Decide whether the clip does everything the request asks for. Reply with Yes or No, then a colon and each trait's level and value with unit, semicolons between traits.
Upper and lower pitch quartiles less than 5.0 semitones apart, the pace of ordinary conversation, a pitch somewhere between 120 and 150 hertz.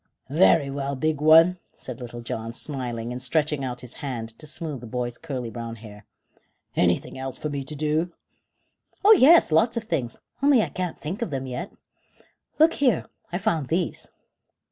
No: wide, 5.4 semitones; average, 175 wpm; medium, 140 Hz